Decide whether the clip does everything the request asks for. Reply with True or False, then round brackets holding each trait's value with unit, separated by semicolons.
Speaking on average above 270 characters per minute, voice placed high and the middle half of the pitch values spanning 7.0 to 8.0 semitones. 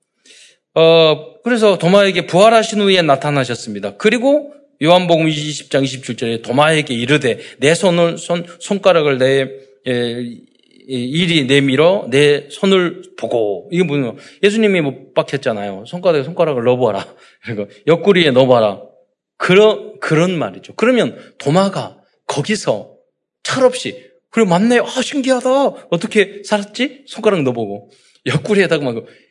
False (290 characters per minute; 170 Hz; 7.4 semitones)